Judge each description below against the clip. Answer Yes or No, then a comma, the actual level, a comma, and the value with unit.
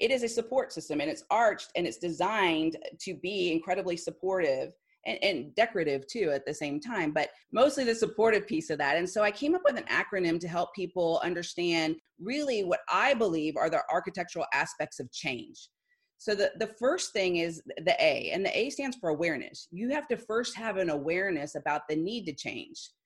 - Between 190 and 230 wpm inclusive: Yes, fast, 205 wpm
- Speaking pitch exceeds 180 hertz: Yes, high, 190 Hz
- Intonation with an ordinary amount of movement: No, wide, 8.0 semitones